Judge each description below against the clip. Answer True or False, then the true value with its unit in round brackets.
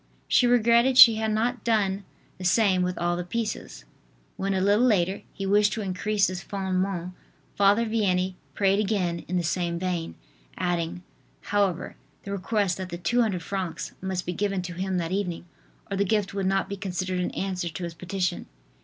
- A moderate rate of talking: True (180 wpm)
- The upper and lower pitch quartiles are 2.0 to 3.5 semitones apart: True (2.4 semitones)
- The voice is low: False (190 Hz)